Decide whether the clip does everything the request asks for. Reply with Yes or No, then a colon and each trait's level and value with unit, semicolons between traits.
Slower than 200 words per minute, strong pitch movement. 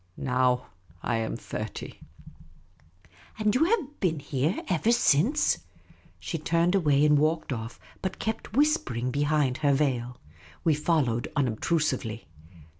Yes: slow, 135 wpm; wide, 5.7 semitones